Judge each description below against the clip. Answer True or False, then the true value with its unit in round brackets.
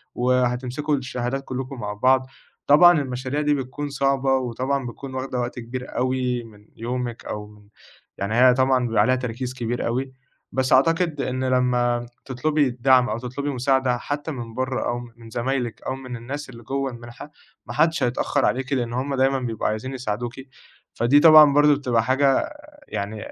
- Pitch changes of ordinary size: False (2.1 semitones)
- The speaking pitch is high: False (130 Hz)